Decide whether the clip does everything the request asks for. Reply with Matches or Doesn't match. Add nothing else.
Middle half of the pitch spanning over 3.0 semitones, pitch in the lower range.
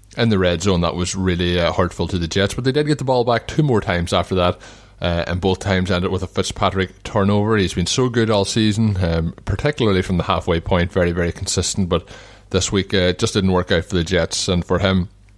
Doesn't match